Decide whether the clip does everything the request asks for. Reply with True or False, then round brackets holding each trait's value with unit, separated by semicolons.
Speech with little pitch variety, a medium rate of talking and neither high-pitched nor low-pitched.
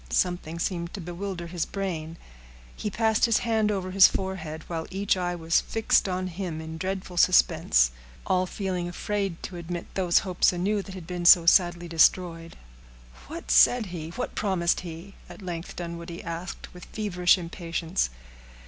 True (2.3 semitones; 155 wpm; 175 Hz)